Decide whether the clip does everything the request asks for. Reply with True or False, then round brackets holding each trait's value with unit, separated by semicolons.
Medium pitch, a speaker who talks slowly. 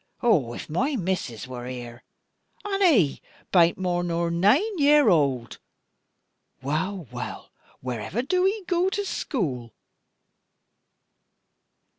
True (175 Hz; 115 wpm)